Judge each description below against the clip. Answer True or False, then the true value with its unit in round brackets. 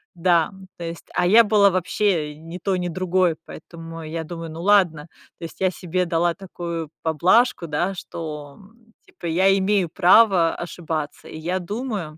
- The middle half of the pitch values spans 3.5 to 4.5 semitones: False (2.6 semitones)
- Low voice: False (175 Hz)